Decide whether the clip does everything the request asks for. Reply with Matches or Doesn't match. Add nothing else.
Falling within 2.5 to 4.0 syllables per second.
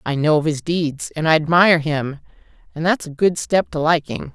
Doesn't match